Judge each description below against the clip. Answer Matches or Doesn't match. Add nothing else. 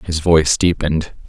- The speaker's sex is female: Doesn't match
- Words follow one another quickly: Doesn't match